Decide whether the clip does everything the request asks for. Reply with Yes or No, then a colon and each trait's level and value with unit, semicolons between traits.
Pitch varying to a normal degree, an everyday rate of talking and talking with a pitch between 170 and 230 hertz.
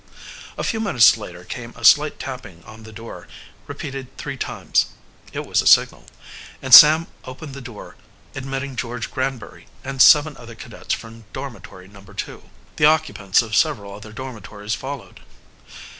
No: average, 4.1 semitones; average, 155 wpm; low, 125 Hz